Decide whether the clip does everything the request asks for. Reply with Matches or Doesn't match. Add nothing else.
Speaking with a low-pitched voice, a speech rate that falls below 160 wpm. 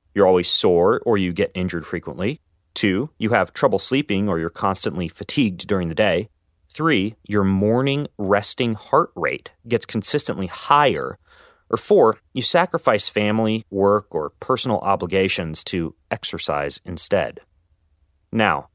Matches